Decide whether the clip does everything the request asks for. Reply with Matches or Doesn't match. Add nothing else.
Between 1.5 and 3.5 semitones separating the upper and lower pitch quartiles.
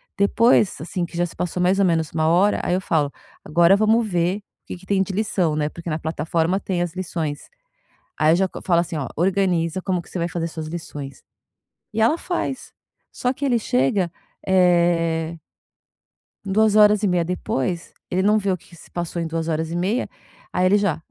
Matches